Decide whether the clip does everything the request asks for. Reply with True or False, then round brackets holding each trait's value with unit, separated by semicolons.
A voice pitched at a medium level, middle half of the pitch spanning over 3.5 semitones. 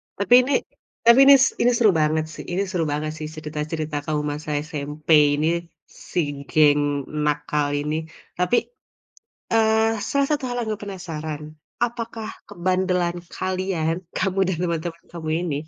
True (165 Hz; 4.5 semitones)